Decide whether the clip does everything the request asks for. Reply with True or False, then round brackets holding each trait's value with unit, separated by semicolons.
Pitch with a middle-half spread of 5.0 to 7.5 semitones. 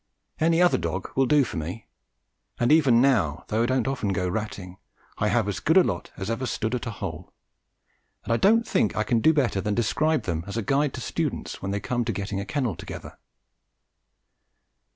True (5.4 semitones)